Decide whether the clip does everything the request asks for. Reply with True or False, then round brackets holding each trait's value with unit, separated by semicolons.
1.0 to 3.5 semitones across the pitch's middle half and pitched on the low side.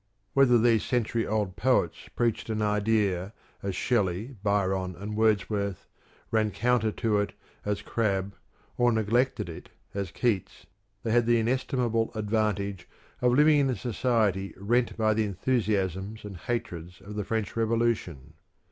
True (3.0 semitones; 110 Hz)